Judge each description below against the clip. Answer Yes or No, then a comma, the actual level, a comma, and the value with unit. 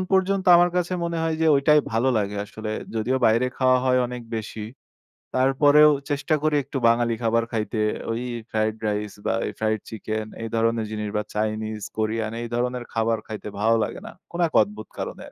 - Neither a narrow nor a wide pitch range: Yes, average, 3.7 semitones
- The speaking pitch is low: Yes, low, 115 Hz